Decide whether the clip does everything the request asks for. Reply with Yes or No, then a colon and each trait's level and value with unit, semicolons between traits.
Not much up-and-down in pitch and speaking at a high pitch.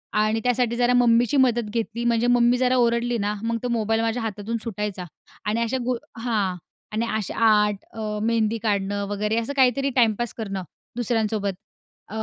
Yes: narrow, 2.2 semitones; high, 230 Hz